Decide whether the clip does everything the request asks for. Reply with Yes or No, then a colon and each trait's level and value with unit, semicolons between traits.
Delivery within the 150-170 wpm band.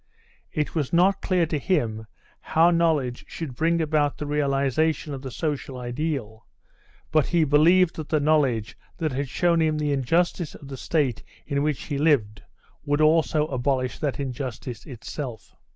Yes: average, 160 wpm